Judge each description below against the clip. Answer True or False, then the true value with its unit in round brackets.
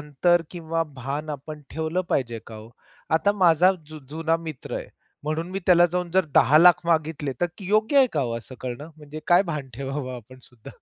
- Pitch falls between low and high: True (155 Hz)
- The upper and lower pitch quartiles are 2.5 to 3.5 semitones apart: False (4.2 semitones)